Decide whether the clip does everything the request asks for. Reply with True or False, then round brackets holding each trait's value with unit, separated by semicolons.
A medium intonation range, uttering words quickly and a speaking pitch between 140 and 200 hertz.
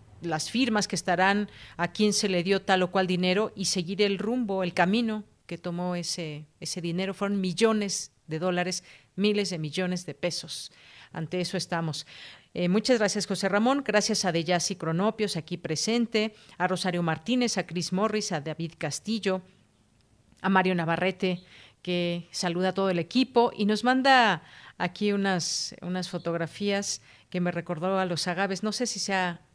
False (3.0 semitones; 170 wpm; 185 Hz)